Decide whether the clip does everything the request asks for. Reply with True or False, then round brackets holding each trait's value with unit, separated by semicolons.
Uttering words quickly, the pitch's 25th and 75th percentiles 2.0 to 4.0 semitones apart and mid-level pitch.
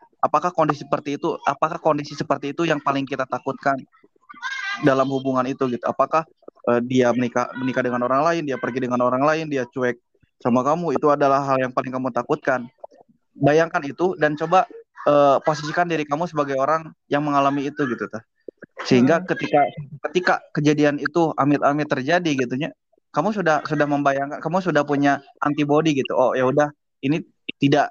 True (165 wpm; 3.1 semitones; 145 Hz)